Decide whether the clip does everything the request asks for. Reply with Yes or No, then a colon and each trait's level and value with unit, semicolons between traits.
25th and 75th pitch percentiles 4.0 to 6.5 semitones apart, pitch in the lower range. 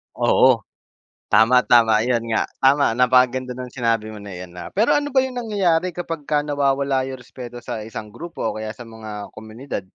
Yes: average, 4.6 semitones; low, 125 Hz